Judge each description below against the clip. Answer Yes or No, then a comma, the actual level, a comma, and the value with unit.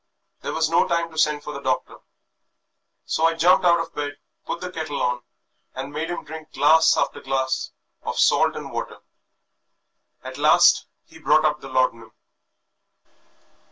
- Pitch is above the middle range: No, medium, 155 Hz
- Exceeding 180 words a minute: No, average, 160 wpm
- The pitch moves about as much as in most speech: Yes, average, 3.3 semitones